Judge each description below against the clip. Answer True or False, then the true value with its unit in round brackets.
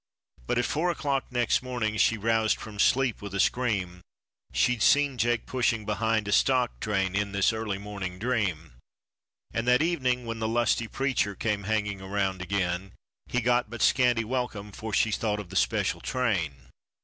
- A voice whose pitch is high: False (110 Hz)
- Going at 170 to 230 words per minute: True (175 wpm)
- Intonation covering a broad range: False (3.6 semitones)